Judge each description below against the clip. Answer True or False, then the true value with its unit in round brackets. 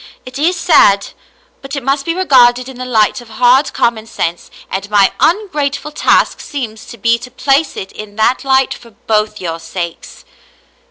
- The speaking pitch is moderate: False (245 Hz)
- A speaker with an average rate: True (175 wpm)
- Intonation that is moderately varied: True (4.6 semitones)